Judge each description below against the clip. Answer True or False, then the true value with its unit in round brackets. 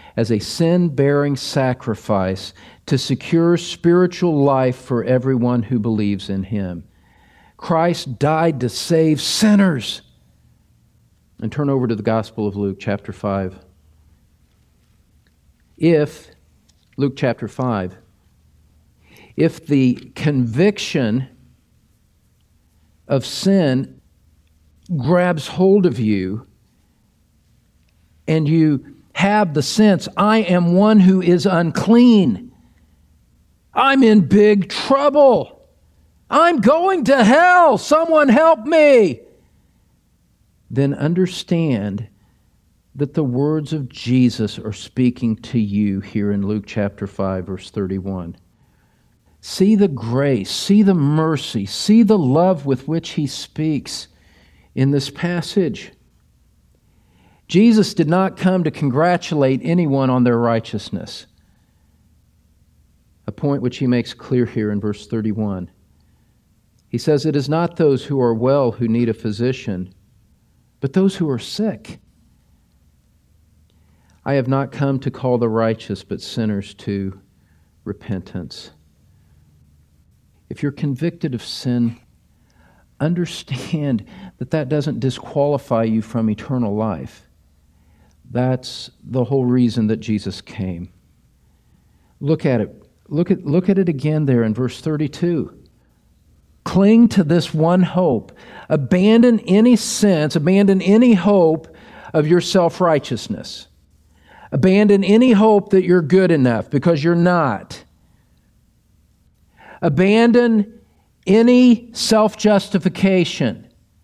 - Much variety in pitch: True (8.9 semitones)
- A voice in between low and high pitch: False (130 Hz)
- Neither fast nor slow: False (110 wpm)